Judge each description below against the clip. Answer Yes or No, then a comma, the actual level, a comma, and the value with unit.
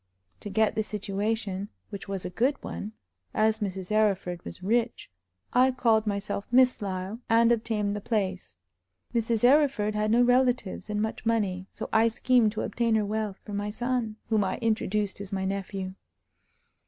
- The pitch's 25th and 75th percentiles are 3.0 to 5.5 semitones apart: No, narrow, 2.5 semitones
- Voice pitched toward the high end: Yes, high, 215 Hz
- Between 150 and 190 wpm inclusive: Yes, average, 165 wpm